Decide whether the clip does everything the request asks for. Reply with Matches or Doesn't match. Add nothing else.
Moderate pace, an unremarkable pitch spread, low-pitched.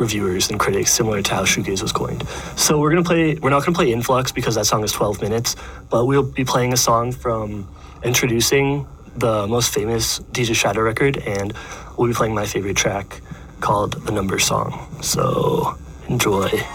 Matches